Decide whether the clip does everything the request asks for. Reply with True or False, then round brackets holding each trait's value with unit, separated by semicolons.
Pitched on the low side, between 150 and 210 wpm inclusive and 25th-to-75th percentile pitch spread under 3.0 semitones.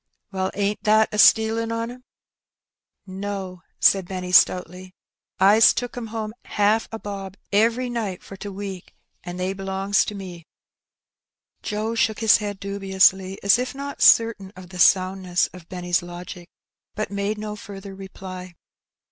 False (195 Hz; 170 wpm; 2.5 semitones)